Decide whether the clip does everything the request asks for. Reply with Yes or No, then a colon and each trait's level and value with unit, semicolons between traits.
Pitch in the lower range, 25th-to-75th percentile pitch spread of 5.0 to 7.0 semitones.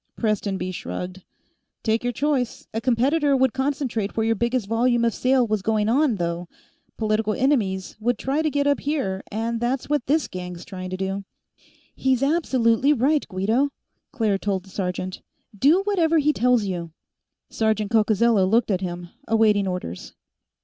No: high, 225 Hz; wide, 5.4 semitones